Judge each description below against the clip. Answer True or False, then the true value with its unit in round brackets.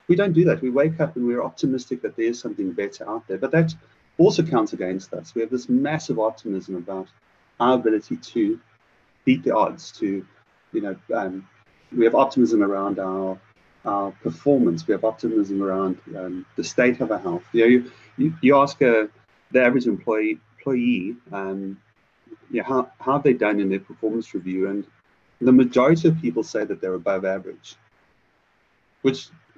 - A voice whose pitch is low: True (115 Hz)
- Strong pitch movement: True (5.7 semitones)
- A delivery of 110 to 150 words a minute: False (185 wpm)